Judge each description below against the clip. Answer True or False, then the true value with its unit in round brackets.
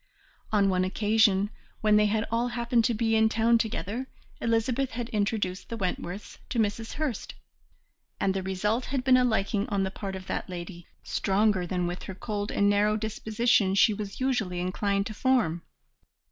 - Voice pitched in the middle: False (210 Hz)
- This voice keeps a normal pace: True (175 wpm)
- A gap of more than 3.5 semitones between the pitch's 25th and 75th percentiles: False (3.0 semitones)